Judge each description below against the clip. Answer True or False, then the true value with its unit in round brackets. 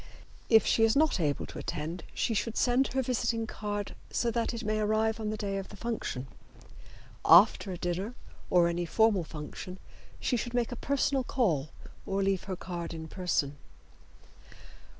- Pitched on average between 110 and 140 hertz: False (210 Hz)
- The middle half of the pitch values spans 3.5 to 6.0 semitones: True (4.8 semitones)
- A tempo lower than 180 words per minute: True (170 wpm)